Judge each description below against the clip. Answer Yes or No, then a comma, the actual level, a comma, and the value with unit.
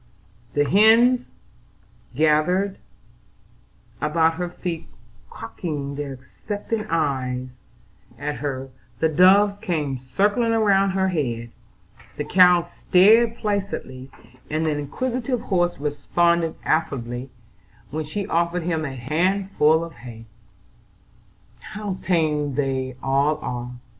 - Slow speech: Yes, slow, 105 wpm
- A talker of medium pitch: Yes, medium, 160 Hz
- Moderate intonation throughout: No, wide, 5.7 semitones